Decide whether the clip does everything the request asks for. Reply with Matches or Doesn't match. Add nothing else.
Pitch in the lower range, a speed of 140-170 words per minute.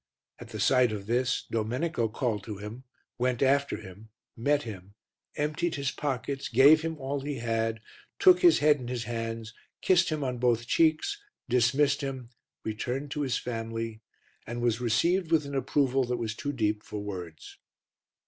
Matches